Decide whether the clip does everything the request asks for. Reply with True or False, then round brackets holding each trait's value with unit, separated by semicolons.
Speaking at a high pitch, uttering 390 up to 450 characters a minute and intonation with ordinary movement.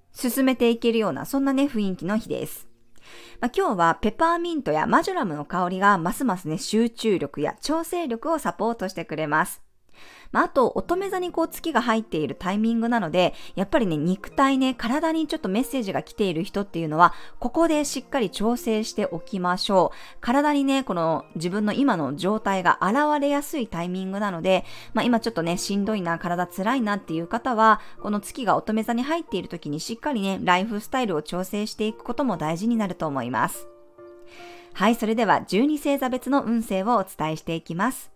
False (215 Hz; 405 characters per minute; 6.5 semitones)